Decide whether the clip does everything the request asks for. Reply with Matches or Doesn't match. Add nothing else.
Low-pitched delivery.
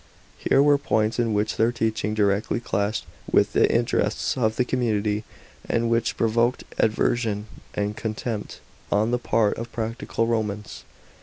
Matches